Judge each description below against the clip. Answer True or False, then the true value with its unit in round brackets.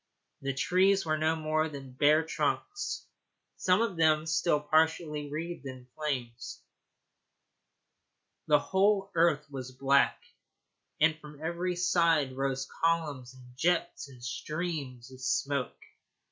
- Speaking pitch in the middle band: True (155 Hz)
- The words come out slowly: True (120 wpm)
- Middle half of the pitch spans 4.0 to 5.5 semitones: False (3.6 semitones)